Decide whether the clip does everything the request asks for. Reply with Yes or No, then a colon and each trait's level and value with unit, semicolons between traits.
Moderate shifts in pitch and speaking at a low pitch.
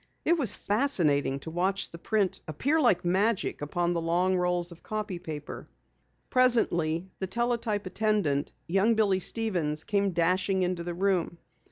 No: average, 3.8 semitones; medium, 185 Hz